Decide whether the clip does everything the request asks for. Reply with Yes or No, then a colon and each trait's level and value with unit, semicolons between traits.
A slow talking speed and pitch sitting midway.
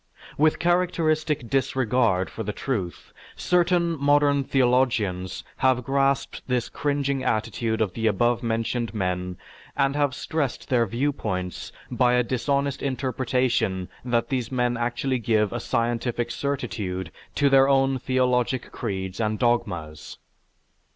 No: slow, 125 wpm; low, 125 Hz